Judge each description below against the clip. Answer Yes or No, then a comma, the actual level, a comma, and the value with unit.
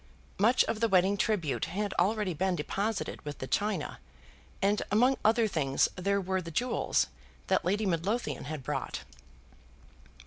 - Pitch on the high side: Yes, high, 195 Hz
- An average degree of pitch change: Yes, average, 3.7 semitones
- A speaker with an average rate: Yes, average, 145 wpm